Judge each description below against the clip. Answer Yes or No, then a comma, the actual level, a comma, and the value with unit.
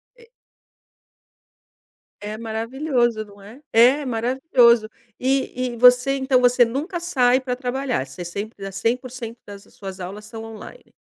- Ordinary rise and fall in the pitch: Yes, average, 3.3 semitones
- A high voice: Yes, high, 245 Hz